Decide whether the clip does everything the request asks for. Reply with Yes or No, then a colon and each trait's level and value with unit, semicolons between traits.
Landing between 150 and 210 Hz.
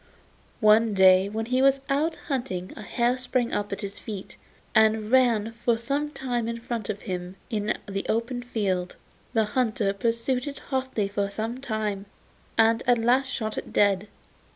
No: high, 225 Hz